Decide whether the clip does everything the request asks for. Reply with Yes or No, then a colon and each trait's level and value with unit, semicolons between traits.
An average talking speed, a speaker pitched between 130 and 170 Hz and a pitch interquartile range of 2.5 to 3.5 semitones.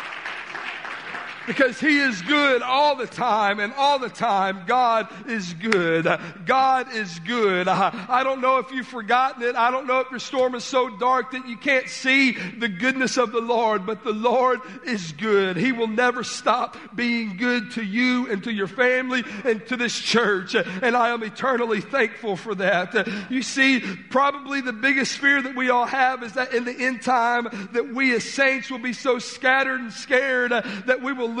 No: average, 195 wpm; high, 245 Hz; average, 2.8 semitones